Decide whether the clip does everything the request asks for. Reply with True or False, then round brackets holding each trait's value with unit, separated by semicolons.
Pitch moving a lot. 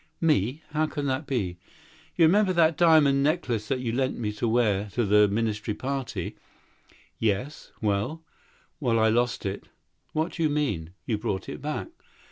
True (6.2 semitones)